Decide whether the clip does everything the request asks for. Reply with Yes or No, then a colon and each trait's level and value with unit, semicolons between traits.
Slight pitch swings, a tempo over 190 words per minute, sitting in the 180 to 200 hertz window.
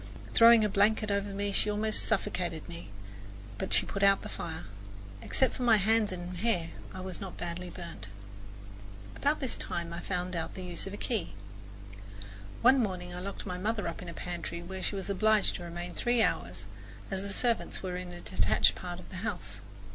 No: average, 3.3 semitones; average, 200 wpm; medium, 185 Hz